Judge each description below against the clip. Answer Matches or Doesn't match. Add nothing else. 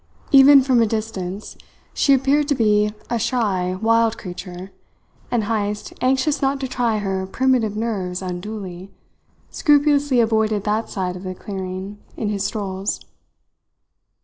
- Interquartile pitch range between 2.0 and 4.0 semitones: Doesn't match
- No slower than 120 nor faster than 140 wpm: Matches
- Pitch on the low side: Doesn't match